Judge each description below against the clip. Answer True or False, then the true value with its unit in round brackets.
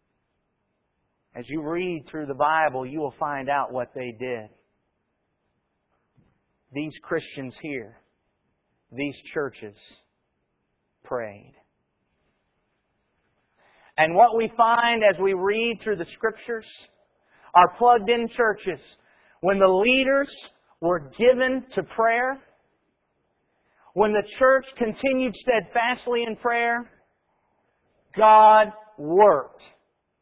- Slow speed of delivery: True (95 wpm)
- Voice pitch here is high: True (210 Hz)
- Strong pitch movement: True (7.3 semitones)